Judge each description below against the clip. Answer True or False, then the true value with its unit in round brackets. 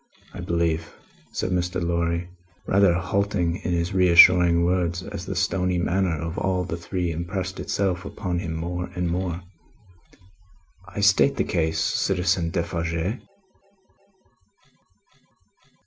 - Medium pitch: False (90 Hz)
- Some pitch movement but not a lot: False (1.6 semitones)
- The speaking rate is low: True (120 wpm)